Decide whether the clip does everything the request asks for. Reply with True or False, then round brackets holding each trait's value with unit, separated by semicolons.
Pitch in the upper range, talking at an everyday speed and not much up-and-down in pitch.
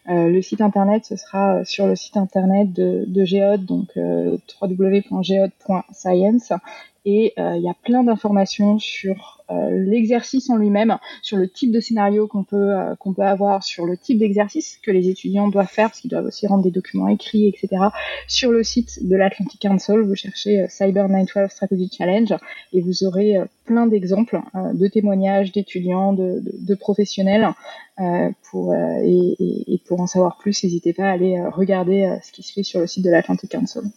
True (195 Hz; 195 wpm; 2.0 semitones)